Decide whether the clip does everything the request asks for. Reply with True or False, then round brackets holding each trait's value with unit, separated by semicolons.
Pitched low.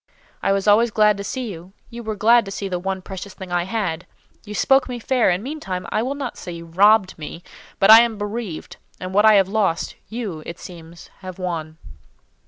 False (195 Hz)